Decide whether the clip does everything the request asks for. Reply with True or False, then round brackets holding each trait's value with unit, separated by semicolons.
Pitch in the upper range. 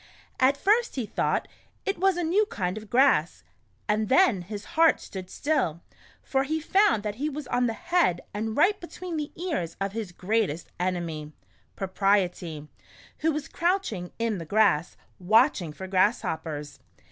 True (220 Hz)